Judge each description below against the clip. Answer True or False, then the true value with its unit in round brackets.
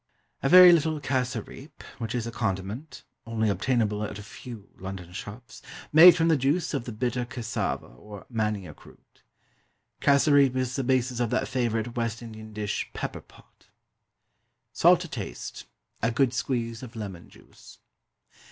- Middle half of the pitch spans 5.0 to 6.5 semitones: False (3.7 semitones)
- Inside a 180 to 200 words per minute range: False (150 wpm)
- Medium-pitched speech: False (120 Hz)